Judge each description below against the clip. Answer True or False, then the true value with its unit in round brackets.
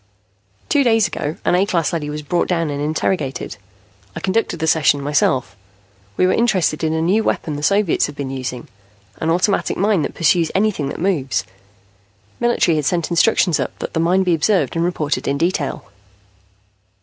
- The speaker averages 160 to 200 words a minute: True (180 wpm)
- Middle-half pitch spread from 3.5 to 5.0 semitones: True (4.1 semitones)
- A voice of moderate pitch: True (165 Hz)